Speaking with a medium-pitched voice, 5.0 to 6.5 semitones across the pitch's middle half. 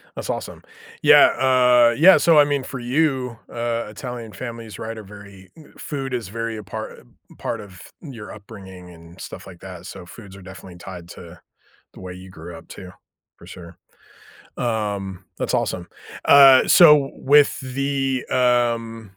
No: low, 115 Hz; wide, 5.4 semitones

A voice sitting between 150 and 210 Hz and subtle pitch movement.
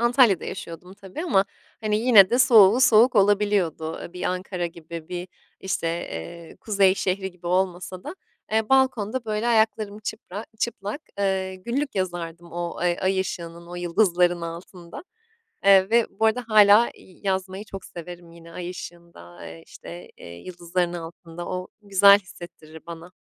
No: medium, 185 Hz; average, 3.4 semitones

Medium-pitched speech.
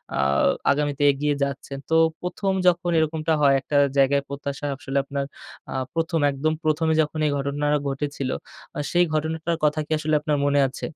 Yes: medium, 150 Hz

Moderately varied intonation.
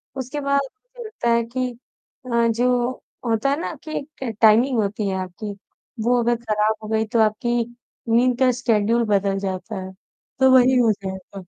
Yes: average, 3.1 semitones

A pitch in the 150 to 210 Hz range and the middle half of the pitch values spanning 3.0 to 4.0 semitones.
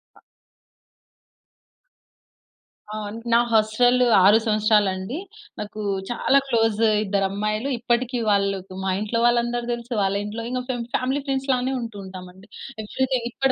No: high, 225 Hz; average, 3.3 semitones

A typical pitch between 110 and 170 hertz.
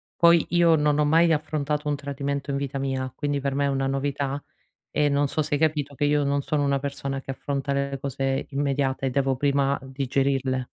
Yes: medium, 140 Hz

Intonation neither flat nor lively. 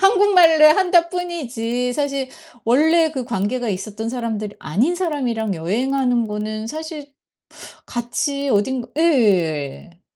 No: wide, 6.5 semitones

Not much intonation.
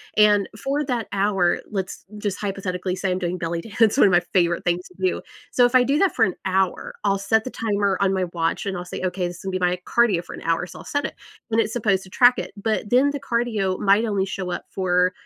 No: average, 3.4 semitones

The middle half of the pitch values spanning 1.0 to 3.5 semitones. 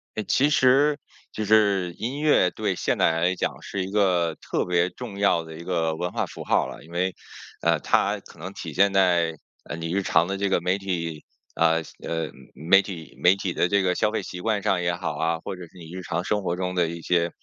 Yes: average, 2.9 semitones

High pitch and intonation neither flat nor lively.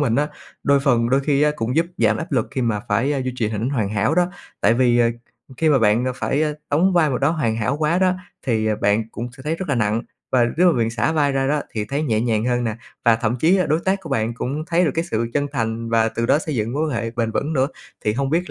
No: low, 125 Hz; average, 4.9 semitones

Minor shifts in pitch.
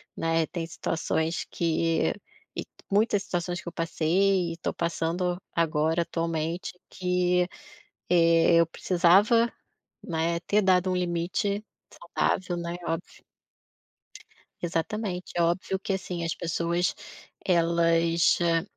Yes: narrow, 1.5 semitones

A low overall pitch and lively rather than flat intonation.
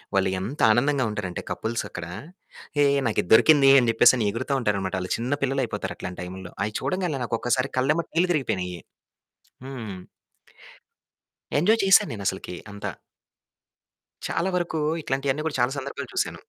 Yes: low, 125 Hz; wide, 6.0 semitones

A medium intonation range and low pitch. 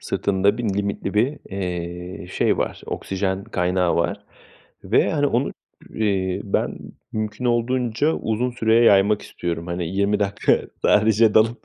Yes: average, 3.1 semitones; low, 100 Hz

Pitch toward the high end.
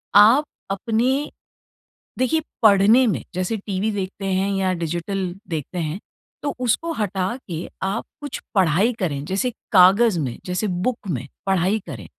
Yes: high, 195 Hz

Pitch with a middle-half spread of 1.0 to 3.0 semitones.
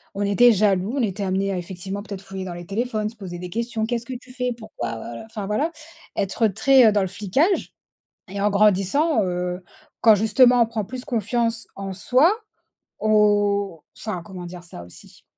No: average, 3.6 semitones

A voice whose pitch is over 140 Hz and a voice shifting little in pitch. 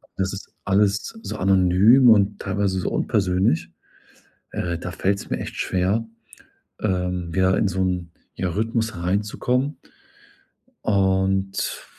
No: very low, 95 Hz; narrow, 2.2 semitones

